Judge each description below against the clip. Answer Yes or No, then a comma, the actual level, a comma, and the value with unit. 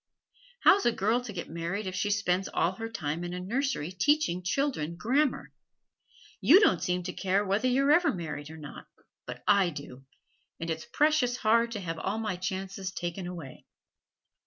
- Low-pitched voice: No, high, 190 Hz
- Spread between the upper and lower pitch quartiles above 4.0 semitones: Yes, wide, 5.4 semitones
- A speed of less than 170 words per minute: No, average, 180 wpm